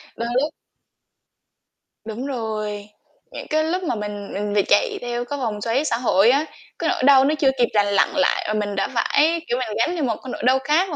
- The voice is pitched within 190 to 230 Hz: No, high, 245 Hz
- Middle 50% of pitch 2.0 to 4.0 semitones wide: No, average, 5.3 semitones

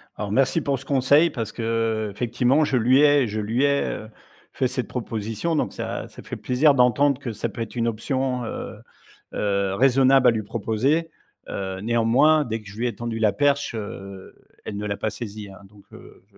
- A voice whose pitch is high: No, low, 120 Hz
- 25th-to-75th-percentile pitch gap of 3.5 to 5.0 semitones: Yes, average, 4.1 semitones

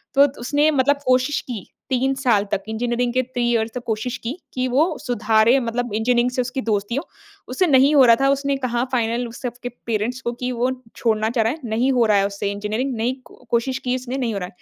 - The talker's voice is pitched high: Yes, high, 245 Hz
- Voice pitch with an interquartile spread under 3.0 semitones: Yes, narrow, 2.4 semitones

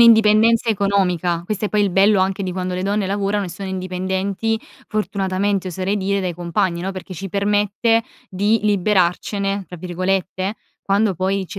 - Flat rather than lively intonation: Yes, narrow, 1.9 semitones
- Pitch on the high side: Yes, high, 195 Hz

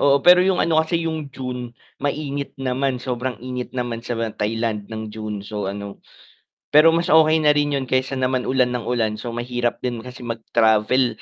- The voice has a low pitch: Yes, low, 125 Hz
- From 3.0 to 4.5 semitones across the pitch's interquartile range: Yes, average, 3.5 semitones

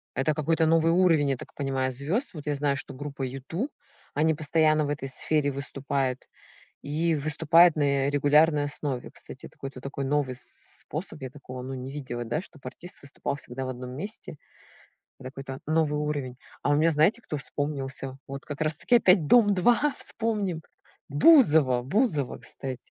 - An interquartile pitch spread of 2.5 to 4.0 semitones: Yes, average, 2.9 semitones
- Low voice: No, medium, 145 Hz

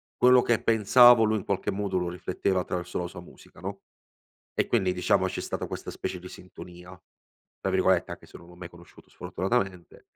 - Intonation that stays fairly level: No, average, 3.1 semitones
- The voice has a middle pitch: No, very low, 95 Hz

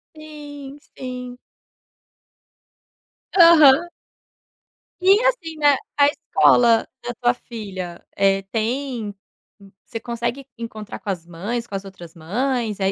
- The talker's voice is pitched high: Yes, high, 240 Hz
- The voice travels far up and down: Yes, wide, 5.7 semitones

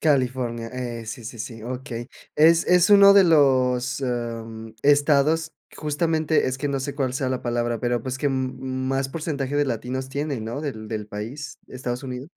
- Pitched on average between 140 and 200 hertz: No, low, 130 Hz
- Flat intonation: No, average, 3.2 semitones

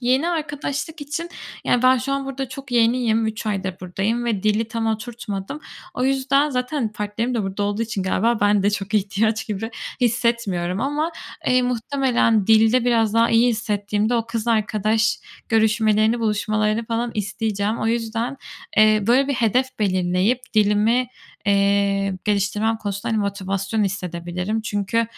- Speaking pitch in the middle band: No, high, 220 Hz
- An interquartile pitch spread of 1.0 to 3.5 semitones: Yes, average, 2.8 semitones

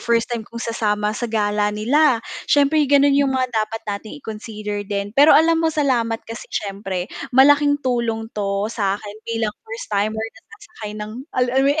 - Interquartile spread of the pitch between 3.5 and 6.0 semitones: Yes, average, 4.2 semitones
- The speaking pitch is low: No, high, 225 Hz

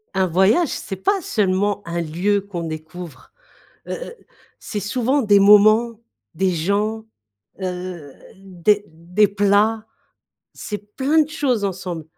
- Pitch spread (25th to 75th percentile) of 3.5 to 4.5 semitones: No, average, 3.1 semitones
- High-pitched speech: Yes, high, 200 Hz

